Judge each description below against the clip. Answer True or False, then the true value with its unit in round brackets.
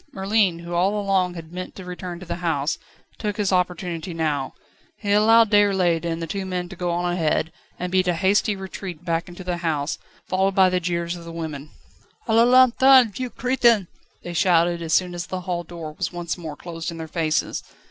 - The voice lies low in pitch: False (180 Hz)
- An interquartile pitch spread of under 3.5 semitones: True (2.5 semitones)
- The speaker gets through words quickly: True (210 wpm)